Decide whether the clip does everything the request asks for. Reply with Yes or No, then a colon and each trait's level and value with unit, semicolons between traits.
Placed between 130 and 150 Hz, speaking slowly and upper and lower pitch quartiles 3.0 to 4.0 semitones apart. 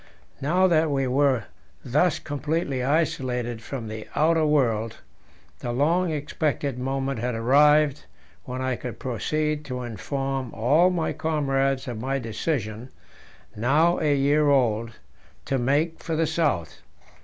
Yes: low, 135 Hz; slow, 130 wpm; average, 3.6 semitones